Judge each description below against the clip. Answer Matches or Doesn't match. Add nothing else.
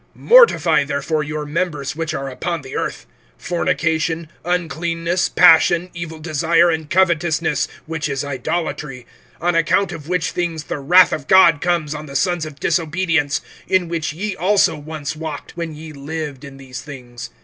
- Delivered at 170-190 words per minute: Doesn't match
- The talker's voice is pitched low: Doesn't match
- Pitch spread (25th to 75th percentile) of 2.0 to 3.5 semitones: Matches